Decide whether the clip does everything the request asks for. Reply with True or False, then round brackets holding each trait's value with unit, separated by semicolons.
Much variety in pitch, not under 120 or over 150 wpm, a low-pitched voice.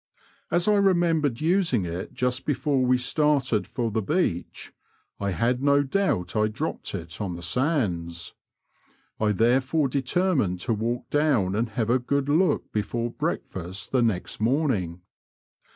True (6.1 semitones; 145 wpm; 125 Hz)